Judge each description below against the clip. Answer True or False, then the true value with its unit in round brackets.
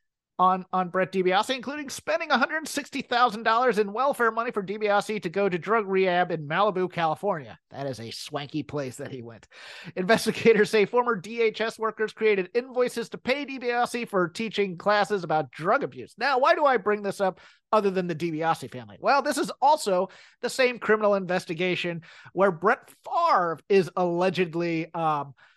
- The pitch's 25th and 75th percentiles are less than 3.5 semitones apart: False (5.2 semitones)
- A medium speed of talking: True (165 wpm)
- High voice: True (200 Hz)